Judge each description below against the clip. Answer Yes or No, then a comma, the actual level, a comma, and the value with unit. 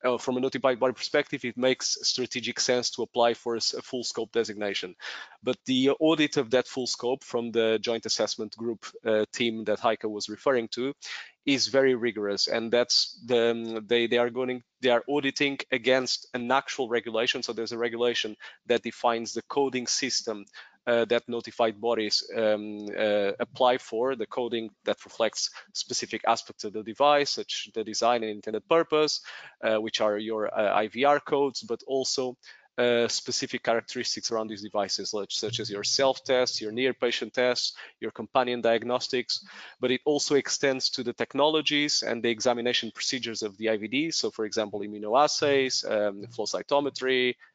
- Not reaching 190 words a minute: Yes, average, 165 wpm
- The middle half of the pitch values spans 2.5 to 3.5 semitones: Yes, average, 2.8 semitones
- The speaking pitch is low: Yes, low, 120 Hz